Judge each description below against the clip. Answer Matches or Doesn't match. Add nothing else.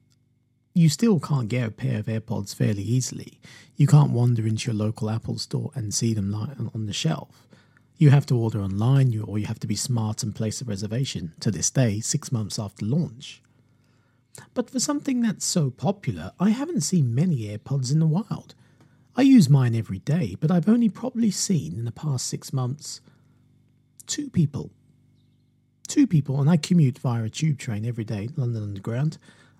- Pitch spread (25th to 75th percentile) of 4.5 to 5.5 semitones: Matches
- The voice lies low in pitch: Matches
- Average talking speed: Matches